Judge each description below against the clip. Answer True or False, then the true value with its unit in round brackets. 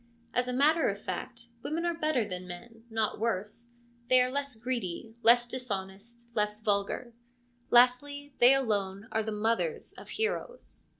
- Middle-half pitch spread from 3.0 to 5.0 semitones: True (3.6 semitones)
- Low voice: False (235 Hz)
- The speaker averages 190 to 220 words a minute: False (155 wpm)